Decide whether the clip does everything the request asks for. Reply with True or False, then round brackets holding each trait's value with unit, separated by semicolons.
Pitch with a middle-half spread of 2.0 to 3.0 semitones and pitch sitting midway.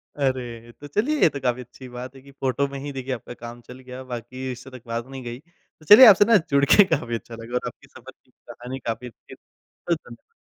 False (2.7 semitones; 130 Hz)